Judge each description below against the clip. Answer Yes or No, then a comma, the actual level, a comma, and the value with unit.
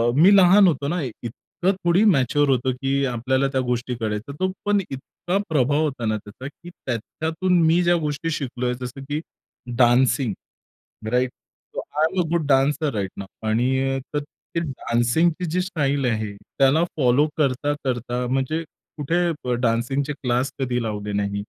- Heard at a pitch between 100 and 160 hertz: Yes, low, 135 Hz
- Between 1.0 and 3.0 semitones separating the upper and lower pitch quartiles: No, average, 4.4 semitones